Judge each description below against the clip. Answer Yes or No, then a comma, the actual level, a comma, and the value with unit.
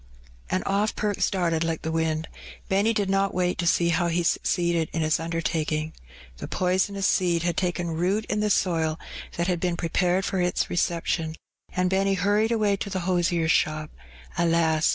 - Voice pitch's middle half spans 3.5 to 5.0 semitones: No, average, 2.7 semitones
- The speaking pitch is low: No, medium, 175 Hz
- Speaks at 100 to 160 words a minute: No, average, 175 wpm